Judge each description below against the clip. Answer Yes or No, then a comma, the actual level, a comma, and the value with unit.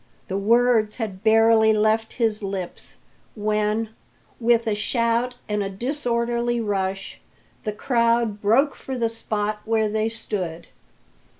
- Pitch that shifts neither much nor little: No, narrow, 1.9 semitones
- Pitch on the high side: Yes, high, 220 Hz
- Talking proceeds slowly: Yes, slow, 125 wpm